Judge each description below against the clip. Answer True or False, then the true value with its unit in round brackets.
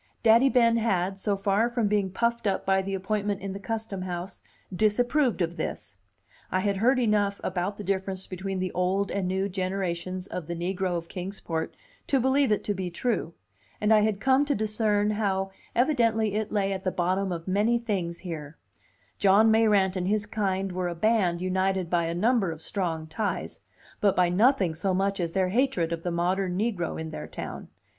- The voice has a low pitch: False (195 Hz)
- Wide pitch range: False (2.8 semitones)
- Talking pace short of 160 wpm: False (195 wpm)